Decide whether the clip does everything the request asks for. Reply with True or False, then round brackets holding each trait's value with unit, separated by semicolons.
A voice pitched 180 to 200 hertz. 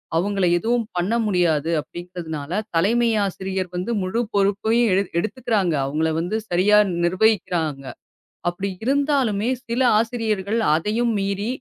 True (195 Hz)